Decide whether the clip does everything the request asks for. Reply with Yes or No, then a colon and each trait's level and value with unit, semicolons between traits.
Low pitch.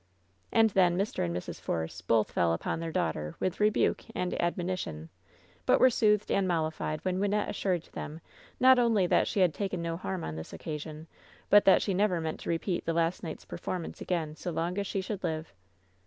No: medium, 175 Hz